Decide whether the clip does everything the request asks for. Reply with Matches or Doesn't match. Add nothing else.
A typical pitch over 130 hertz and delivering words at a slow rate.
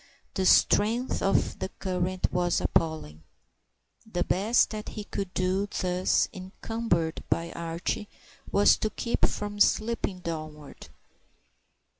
Matches